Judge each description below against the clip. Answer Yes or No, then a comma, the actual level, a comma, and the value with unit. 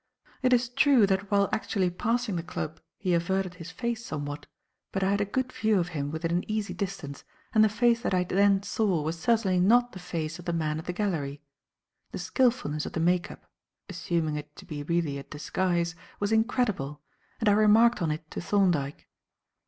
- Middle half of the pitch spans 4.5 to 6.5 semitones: Yes, average, 5.0 semitones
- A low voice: No, medium, 185 Hz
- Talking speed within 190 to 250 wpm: Yes, average, 200 wpm